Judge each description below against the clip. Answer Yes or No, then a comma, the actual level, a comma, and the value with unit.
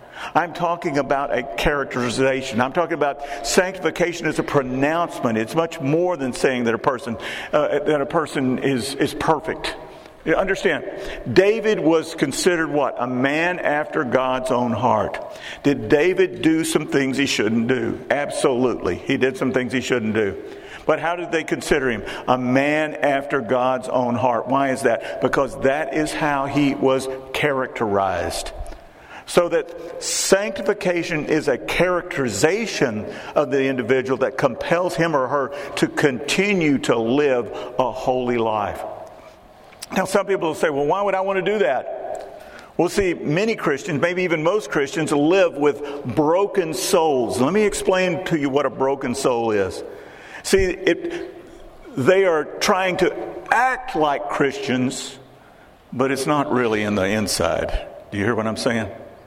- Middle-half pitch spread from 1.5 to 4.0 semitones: No, average, 5.3 semitones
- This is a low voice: No, medium, 145 Hz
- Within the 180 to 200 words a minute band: No, average, 165 wpm